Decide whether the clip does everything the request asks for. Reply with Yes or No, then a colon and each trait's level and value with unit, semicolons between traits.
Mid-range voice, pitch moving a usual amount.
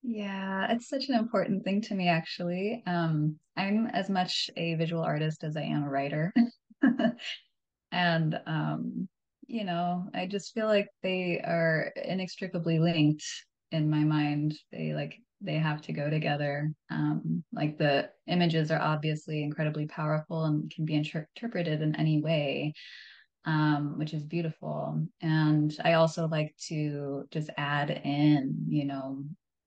Yes: medium, 155 Hz; average, 3.0 semitones